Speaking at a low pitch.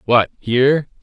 Yes: low, 130 Hz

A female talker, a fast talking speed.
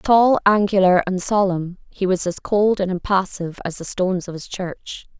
No: female; average, 185 wpm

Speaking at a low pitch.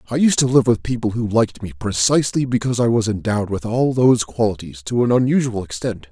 Yes: low, 115 Hz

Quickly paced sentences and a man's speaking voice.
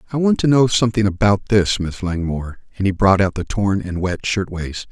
Yes: fast, 220 wpm; male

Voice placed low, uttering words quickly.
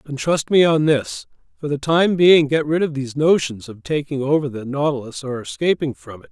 No: medium, 145 Hz; fast, 220 wpm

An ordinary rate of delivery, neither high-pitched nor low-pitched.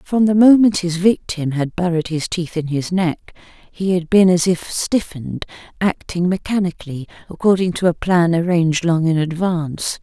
Yes: average, 170 wpm; medium, 175 Hz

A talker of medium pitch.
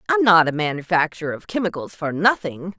Yes: medium, 170 Hz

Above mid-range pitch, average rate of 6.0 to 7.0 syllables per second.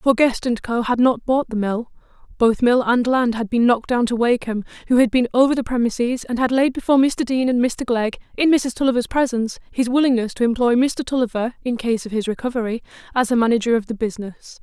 Yes: high, 240 Hz; 6.1 syllables/s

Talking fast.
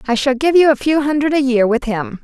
Yes: fast, 295 wpm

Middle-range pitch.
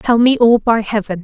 No: high, 220 Hz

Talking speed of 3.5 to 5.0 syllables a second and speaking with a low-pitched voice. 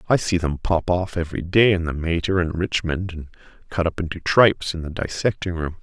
No: 5.6 syllables/s; very low, 85 Hz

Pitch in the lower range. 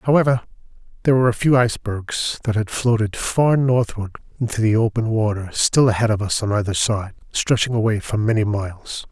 Yes: low, 110 Hz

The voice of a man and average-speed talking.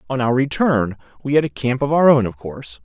No: male; fast, 255 wpm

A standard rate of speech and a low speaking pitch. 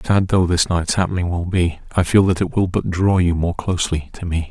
No: fast, 255 wpm; very low, 90 Hz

